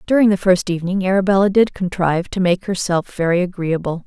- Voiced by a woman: Yes, female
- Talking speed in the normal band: Yes, average, 175 wpm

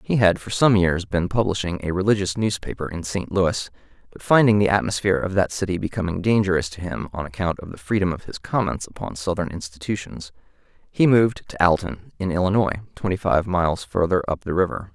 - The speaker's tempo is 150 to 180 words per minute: No, average, 195 wpm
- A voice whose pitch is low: Yes, very low, 95 Hz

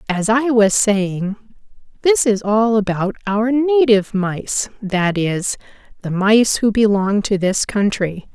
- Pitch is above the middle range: Yes, high, 210 Hz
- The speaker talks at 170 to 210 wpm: No, average, 145 wpm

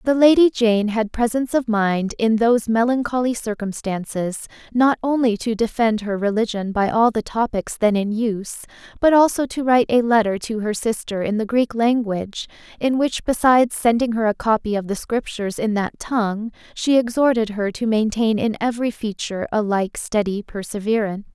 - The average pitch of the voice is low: No, high, 225 Hz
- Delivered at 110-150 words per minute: No, average, 175 wpm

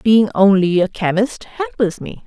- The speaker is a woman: Yes, female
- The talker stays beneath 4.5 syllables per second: Yes, 4.1 syllables/s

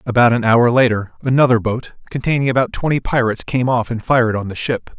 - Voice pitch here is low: Yes, low, 120 Hz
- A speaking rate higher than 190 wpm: Yes, fast, 205 wpm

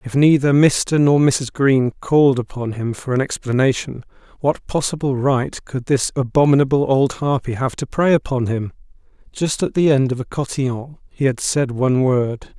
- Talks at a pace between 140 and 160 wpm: No, average, 175 wpm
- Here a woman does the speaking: No, male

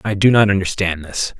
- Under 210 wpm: No, fast, 215 wpm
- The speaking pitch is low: Yes, very low, 95 Hz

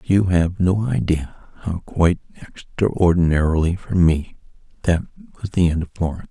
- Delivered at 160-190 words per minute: No, average, 145 wpm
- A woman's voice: No, male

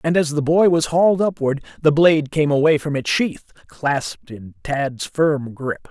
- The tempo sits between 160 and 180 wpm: No, average, 195 wpm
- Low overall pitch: No, medium, 150 Hz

